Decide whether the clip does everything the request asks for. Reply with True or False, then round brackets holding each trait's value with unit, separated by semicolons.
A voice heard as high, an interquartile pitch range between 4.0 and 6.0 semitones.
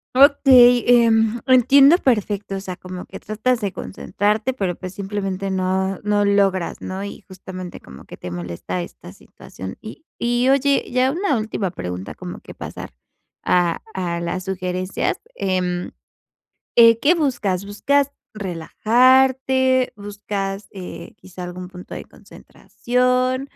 True (205 Hz; 5.4 semitones)